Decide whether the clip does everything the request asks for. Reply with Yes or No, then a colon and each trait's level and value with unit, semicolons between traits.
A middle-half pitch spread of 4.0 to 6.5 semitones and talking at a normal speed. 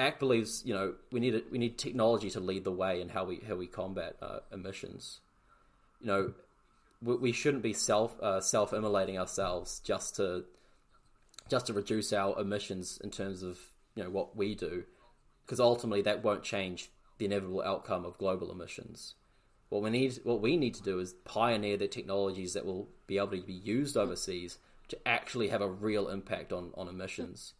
No: average, 3.0 semitones; average, 190 wpm